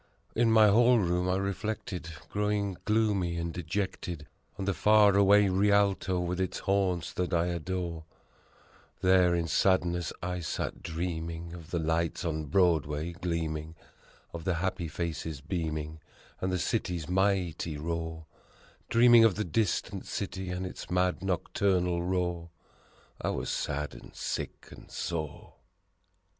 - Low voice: Yes, very low, 90 Hz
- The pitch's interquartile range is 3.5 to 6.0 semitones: No, average, 2.7 semitones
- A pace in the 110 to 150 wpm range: Yes, slow, 135 wpm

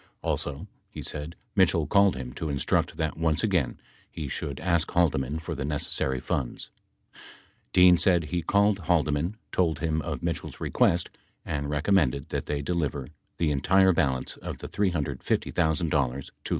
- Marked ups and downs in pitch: No, average, 3.5 semitones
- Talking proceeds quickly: No, average, 150 wpm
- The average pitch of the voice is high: No, very low, 80 Hz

